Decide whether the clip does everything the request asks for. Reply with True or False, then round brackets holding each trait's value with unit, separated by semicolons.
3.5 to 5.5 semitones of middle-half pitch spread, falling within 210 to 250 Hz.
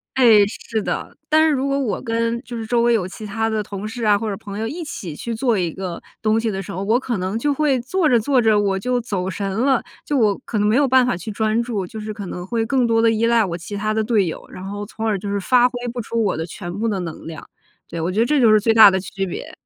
False (3.1 semitones; 220 Hz)